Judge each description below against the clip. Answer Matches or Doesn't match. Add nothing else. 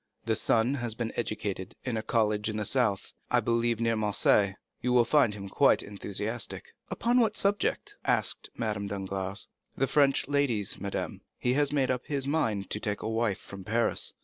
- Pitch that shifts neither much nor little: Matches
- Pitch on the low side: Matches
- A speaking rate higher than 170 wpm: Matches